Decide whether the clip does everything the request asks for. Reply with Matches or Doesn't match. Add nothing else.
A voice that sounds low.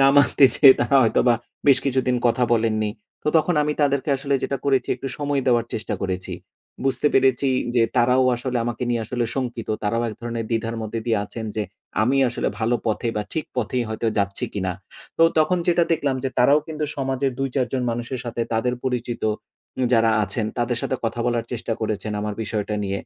Matches